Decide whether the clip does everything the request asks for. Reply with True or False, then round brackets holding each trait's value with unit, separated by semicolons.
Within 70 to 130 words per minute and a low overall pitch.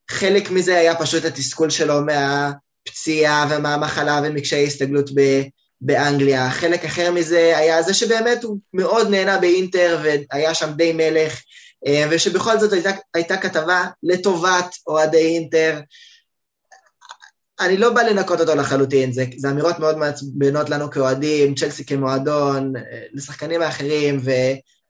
False (125 wpm; 155 Hz)